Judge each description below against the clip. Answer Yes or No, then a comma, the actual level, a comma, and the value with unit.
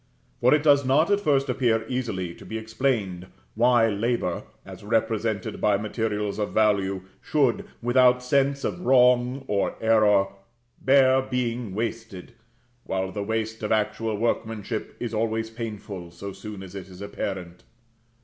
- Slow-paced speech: No, average, 145 wpm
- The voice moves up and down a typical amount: Yes, average, 3.5 semitones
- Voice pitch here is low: Yes, low, 110 Hz